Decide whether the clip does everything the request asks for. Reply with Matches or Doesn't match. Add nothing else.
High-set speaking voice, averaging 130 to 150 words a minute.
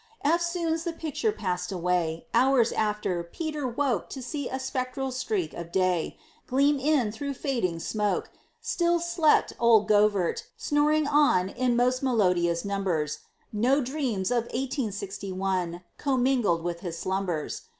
Matches